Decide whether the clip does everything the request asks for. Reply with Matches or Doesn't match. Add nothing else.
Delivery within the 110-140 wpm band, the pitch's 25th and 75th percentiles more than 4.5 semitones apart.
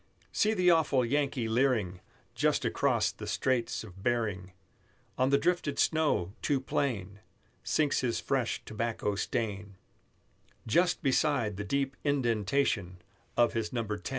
Matches